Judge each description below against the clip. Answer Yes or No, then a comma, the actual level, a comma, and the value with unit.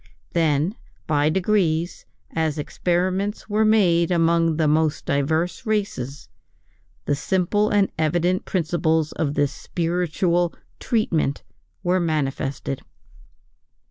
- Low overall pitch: No, medium, 170 Hz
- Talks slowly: Yes, slow, 100 wpm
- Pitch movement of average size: Yes, average, 3.2 semitones